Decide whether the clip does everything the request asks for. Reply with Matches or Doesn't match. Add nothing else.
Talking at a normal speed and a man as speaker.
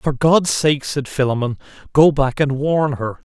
Matches